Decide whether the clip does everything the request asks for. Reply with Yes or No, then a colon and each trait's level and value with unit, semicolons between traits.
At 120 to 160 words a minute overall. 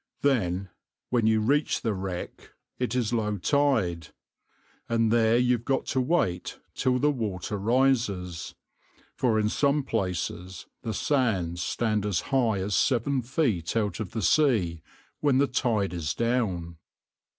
Yes: average, 140 wpm